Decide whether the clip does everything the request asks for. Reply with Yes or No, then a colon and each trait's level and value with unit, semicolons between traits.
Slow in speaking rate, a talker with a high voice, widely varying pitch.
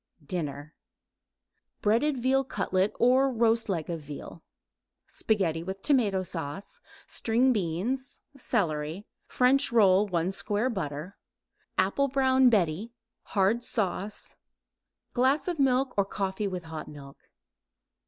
Yes: slow, 110 wpm; high, 205 Hz; wide, 6.5 semitones